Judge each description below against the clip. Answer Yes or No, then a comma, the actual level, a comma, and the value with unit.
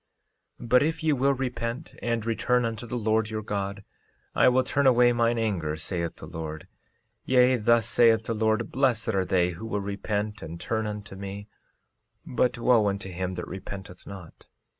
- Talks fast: No, average, 180 wpm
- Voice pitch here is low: Yes, low, 110 Hz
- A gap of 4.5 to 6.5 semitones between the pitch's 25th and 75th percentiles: No, average, 3.6 semitones